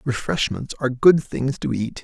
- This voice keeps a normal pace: Yes, average, 175 wpm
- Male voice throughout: Yes, male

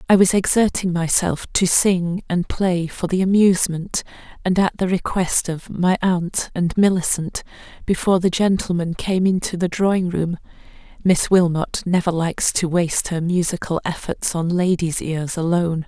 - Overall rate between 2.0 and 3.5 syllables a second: Yes, 3.3 syllables/s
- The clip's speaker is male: No, female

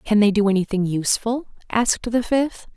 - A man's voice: No, female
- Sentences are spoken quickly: No, average, 175 wpm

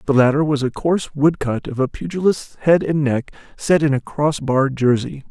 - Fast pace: Yes, fast, 215 wpm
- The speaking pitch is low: No, medium, 145 Hz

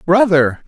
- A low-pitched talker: No, medium, 175 Hz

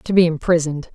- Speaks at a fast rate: No, average, 190 wpm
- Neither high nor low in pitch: Yes, medium, 165 Hz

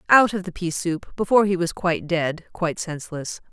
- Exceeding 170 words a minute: Yes, fast, 205 wpm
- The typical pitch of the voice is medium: Yes, medium, 175 Hz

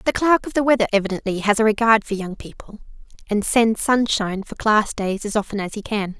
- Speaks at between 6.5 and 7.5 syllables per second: No, 5.8 syllables/s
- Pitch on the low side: No, high, 215 Hz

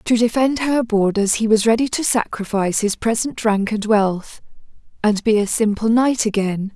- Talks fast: No, average, 180 wpm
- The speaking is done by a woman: Yes, female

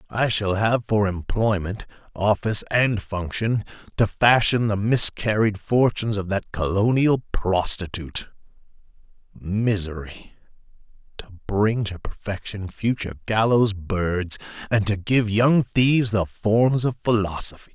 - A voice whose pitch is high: No, low, 105 Hz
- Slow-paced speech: Yes, slow, 115 wpm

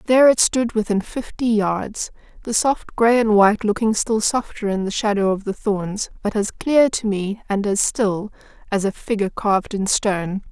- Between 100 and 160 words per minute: No, average, 185 wpm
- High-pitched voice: Yes, high, 210 Hz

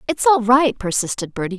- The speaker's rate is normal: Yes, average, 190 wpm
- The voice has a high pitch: Yes, high, 230 Hz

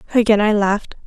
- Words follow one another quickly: No, average, 170 wpm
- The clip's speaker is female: Yes, female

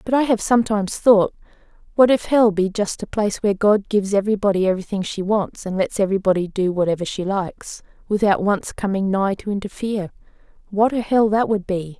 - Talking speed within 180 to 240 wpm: Yes, average, 190 wpm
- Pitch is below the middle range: No, high, 200 Hz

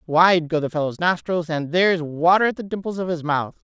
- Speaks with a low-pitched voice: No, medium, 170 Hz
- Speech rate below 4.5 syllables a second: No, 5.5 syllables/s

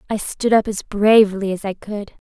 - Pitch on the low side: No, high, 205 Hz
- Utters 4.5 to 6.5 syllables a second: Yes, 5.0 syllables/s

